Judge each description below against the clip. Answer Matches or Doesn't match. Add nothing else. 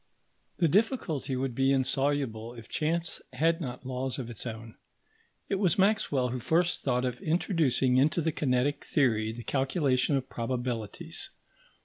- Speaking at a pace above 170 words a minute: Doesn't match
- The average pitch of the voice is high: Doesn't match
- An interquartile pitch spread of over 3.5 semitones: Matches